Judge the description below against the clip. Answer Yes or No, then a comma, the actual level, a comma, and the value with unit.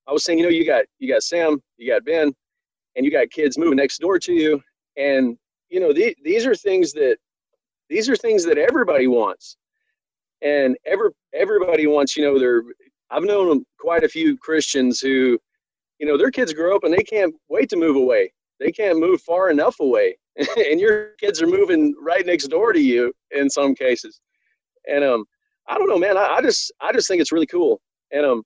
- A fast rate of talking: Yes, fast, 210 wpm